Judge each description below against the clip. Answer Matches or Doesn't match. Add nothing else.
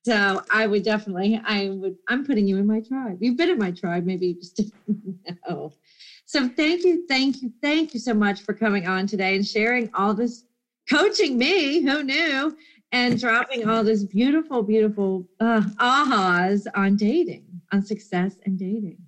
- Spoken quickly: Doesn't match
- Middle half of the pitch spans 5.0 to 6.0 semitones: Doesn't match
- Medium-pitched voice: Doesn't match